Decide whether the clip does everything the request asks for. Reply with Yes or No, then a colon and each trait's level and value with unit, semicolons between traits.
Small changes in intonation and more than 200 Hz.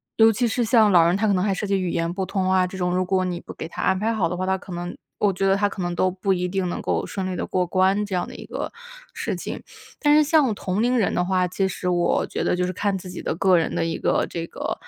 No: narrow, 2.0 semitones; medium, 185 Hz